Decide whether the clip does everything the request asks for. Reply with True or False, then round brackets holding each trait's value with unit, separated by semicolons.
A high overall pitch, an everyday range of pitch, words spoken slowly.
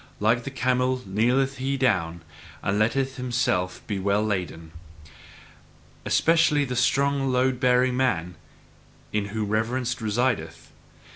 False (125 Hz; 4.0 semitones; 120 wpm)